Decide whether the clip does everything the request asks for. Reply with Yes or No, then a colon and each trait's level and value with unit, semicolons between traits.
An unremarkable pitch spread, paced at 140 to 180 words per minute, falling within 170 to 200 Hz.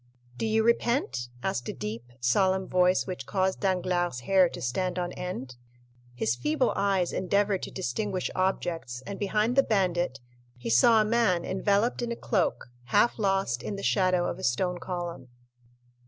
No: wide, 6.9 semitones; average, 165 wpm; medium, 185 Hz